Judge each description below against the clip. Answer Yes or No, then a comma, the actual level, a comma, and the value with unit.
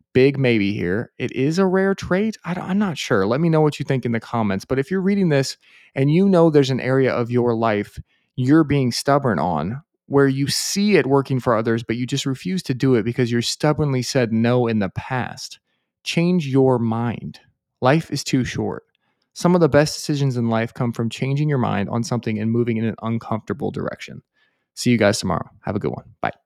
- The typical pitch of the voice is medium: No, low, 130 Hz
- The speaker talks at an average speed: No, fast, 220 wpm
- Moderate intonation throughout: Yes, average, 4.2 semitones